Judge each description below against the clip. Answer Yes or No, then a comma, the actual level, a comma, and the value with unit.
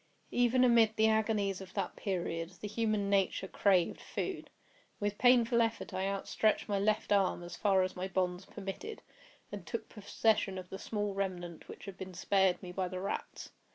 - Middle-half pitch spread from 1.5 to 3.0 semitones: Yes, narrow, 2.6 semitones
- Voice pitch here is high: Yes, high, 195 Hz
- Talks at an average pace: Yes, average, 180 wpm